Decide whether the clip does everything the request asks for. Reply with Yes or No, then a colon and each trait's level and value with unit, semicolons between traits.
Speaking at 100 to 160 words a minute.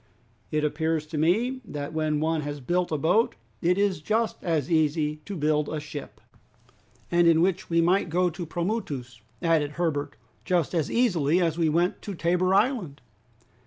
No: average, 175 wpm